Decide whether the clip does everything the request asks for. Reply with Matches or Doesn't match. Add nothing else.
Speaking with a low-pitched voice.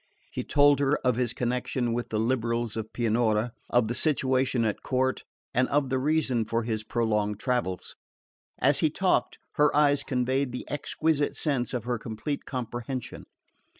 Matches